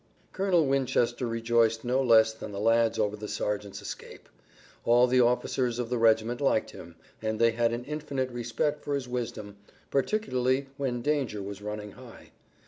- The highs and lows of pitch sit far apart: No, average, 2.9 semitones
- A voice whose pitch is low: Yes, low, 120 Hz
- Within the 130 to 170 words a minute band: Yes, average, 165 wpm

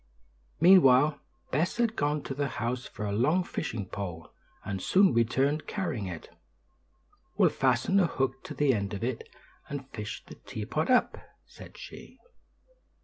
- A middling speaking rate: Yes, average, 150 wpm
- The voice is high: No, low, 135 Hz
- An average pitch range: No, wide, 6.1 semitones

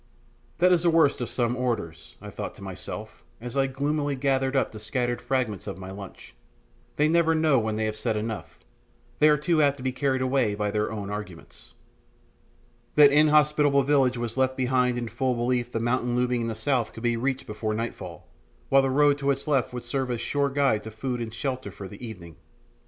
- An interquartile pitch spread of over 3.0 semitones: Yes, average, 4.0 semitones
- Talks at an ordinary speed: No, fast, 210 wpm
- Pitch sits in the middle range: No, low, 125 Hz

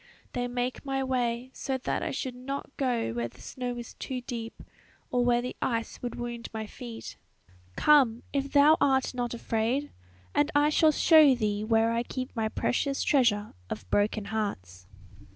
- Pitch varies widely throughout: No, average, 2.9 semitones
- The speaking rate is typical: Yes, average, 170 wpm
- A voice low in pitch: No, high, 245 Hz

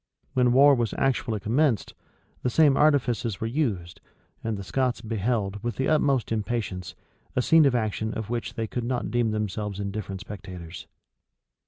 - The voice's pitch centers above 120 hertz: No, low, 115 Hz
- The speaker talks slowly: No, average, 165 wpm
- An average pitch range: Yes, average, 3.6 semitones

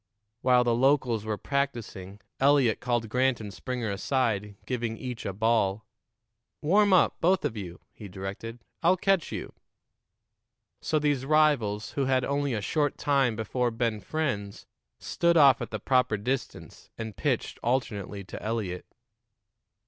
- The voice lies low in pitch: Yes, low, 120 Hz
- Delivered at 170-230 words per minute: No, average, 145 wpm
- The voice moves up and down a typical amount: Yes, average, 4.6 semitones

